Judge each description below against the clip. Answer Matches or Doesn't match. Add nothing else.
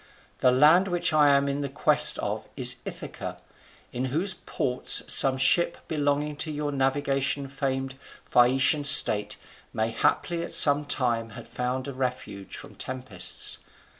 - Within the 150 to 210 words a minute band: Doesn't match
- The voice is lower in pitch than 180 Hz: Matches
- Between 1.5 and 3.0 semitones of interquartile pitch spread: Matches